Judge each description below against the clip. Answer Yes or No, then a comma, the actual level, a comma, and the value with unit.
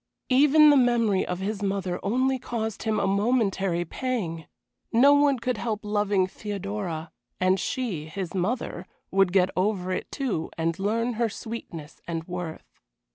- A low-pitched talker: No, high, 200 Hz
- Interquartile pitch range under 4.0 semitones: No, average, 4.6 semitones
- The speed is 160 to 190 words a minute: No, average, 150 wpm